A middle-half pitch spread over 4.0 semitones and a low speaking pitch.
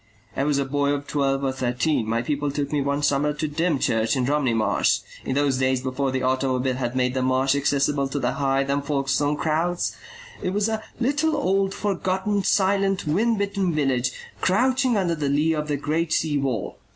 No: average, 4.5 semitones; medium, 145 Hz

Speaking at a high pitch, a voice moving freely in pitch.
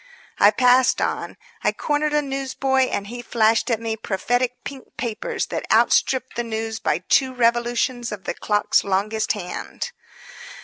No: high, 240 Hz; average, 3.0 semitones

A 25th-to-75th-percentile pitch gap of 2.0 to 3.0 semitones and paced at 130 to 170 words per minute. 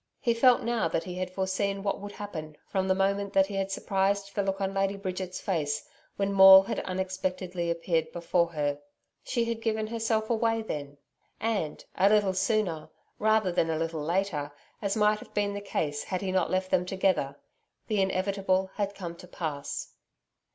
No: narrow, 2.4 semitones; average, 185 wpm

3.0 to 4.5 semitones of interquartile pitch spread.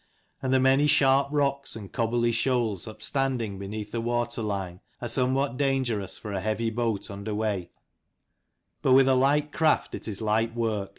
Yes: average, 3.9 semitones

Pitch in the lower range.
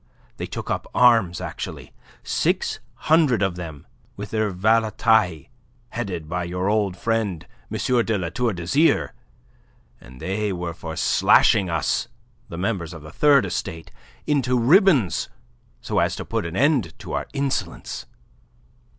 Yes: low, 100 Hz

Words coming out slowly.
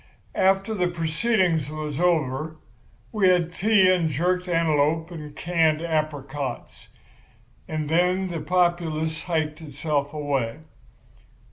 Yes: slow, 110 wpm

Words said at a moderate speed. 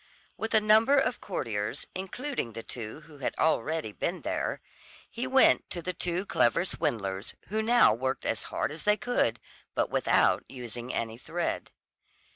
Yes: average, 160 wpm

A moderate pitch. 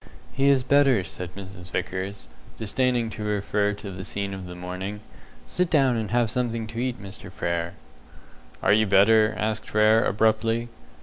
No: low, 105 Hz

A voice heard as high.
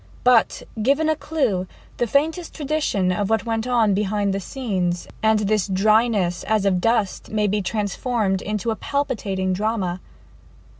Yes: high, 215 Hz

